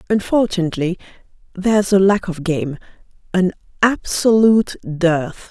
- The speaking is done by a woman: Yes, female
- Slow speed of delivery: Yes, slow, 100 wpm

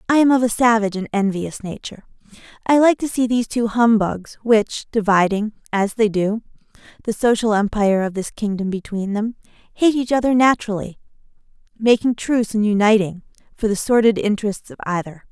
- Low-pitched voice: No, high, 215 Hz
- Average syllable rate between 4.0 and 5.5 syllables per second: No, 5.7 syllables/s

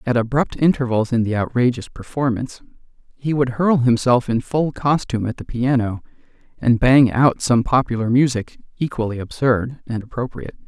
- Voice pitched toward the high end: No, low, 125 Hz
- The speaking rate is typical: Yes, average, 150 wpm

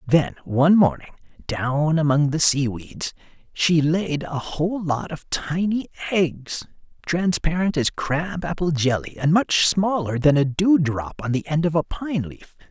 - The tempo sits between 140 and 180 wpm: Yes, average, 165 wpm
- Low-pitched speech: No, medium, 155 Hz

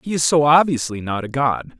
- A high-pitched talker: No, low, 135 Hz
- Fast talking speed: Yes, fast, 235 wpm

